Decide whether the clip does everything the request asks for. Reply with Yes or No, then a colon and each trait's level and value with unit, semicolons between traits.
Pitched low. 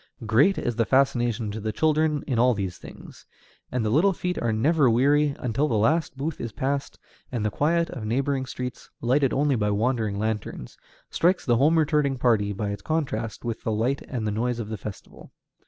Yes: low, 125 Hz